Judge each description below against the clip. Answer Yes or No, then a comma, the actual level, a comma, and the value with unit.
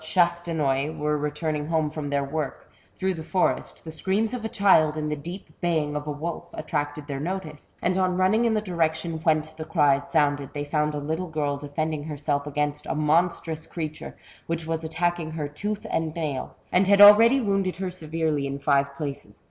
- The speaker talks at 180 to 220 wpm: Yes, average, 190 wpm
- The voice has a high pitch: No, medium, 155 Hz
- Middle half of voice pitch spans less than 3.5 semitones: Yes, average, 2.8 semitones